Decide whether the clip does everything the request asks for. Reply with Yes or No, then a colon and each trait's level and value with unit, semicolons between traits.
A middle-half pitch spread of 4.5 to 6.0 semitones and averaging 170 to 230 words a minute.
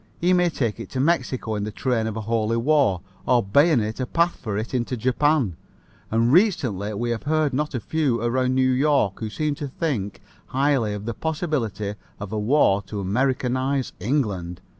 Yes: average, 5.1 semitones; average, 185 wpm